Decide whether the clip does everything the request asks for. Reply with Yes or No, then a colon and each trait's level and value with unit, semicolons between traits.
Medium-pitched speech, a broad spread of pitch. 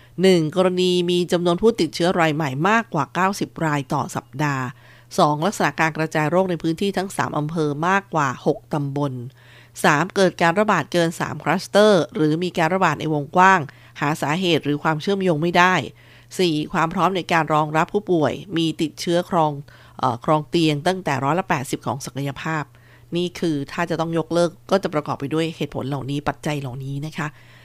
No: medium, 160 Hz; average, 3.6 semitones